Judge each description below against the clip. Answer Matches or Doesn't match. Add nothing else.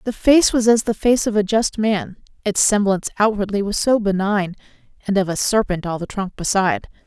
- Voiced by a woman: Matches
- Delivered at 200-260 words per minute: Matches